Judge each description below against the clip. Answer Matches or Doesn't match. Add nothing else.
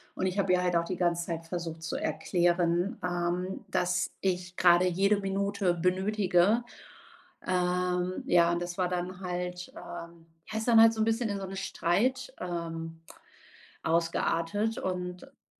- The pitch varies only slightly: Matches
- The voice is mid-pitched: Matches